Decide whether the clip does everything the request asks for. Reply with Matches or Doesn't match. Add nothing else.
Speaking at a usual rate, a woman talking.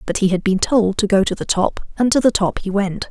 Doesn't match